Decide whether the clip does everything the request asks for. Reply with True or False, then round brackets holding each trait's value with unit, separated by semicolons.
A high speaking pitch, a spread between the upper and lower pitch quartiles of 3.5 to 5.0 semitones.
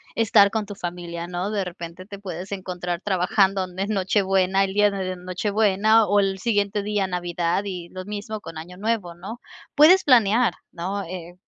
False (195 Hz; 2.5 semitones)